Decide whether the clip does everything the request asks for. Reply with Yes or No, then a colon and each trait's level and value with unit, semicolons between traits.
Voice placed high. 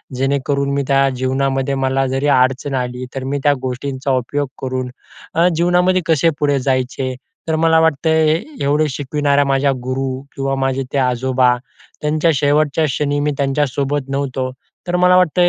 No: medium, 140 Hz